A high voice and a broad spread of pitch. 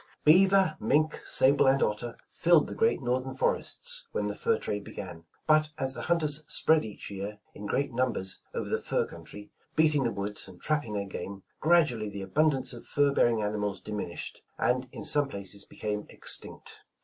No: low, 130 Hz; wide, 6.8 semitones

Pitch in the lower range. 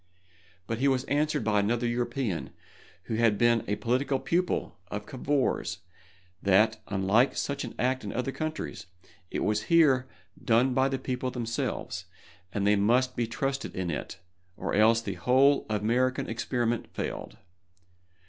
Yes: low, 120 Hz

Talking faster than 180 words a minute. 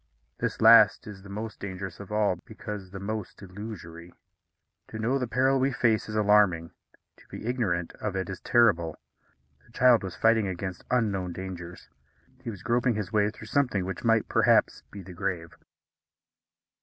No: average, 170 wpm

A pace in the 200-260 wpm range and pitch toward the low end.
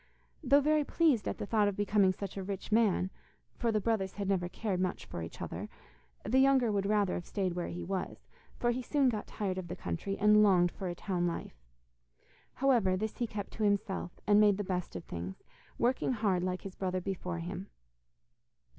No: fast, 205 wpm; high, 200 Hz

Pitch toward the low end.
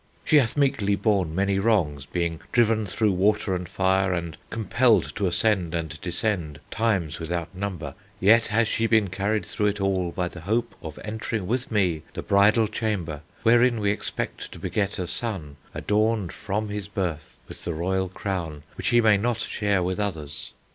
Yes: low, 100 Hz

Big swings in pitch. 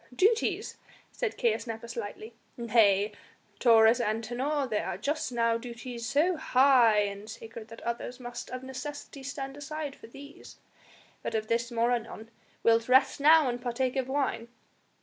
No: average, 3.0 semitones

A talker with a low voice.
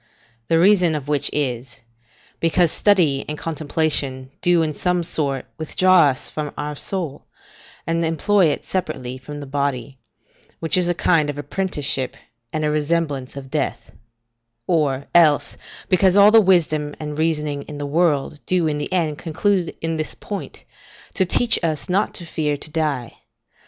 No: medium, 155 Hz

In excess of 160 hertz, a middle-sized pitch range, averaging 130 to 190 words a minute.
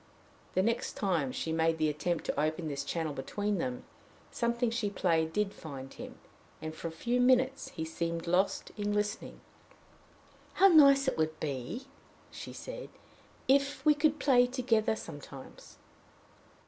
No: high, 190 Hz; wide, 7.7 semitones; average, 150 wpm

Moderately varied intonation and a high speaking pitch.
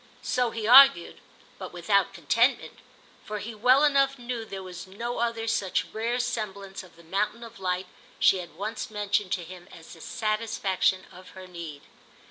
Yes: average, 4.0 semitones; high, 210 Hz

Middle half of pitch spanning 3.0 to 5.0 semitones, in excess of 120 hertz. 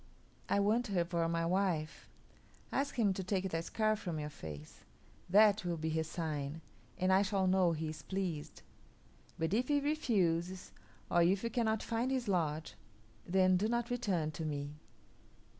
Yes: average, 4.6 semitones; medium, 185 Hz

